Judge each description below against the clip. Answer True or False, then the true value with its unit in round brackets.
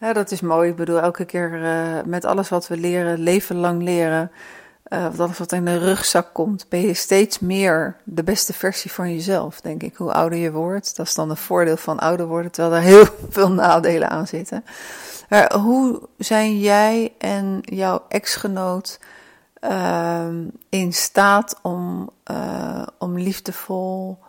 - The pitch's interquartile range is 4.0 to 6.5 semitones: False (2.8 semitones)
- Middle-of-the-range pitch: True (180 Hz)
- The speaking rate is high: False (170 wpm)